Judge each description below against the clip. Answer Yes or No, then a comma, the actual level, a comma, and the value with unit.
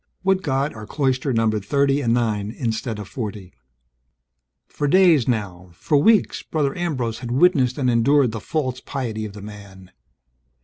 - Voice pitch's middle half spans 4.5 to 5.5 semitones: Yes, average, 4.8 semitones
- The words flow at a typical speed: Yes, average, 160 wpm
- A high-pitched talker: No, low, 125 Hz